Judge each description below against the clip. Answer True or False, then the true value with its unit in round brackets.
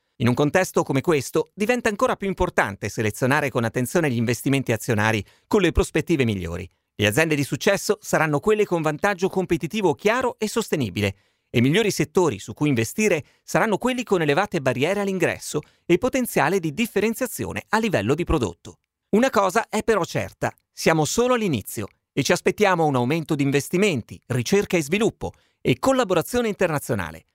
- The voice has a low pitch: False (160 Hz)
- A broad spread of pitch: True (8.8 semitones)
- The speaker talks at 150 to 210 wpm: True (160 wpm)